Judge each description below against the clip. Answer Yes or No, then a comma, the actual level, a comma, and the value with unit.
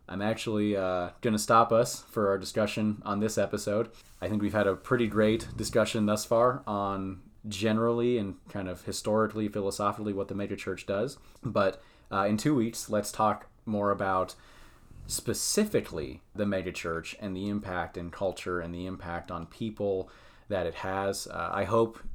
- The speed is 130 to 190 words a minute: Yes, average, 165 wpm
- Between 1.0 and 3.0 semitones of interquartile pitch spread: Yes, narrow, 2.5 semitones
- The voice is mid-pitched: No, low, 105 Hz